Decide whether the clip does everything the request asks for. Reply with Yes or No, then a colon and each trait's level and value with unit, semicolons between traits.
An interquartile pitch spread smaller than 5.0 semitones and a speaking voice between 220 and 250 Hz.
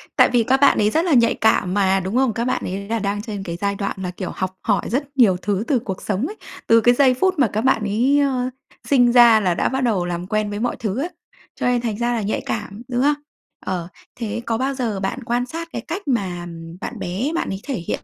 Yes: average, 4.5 semitones; high, 225 Hz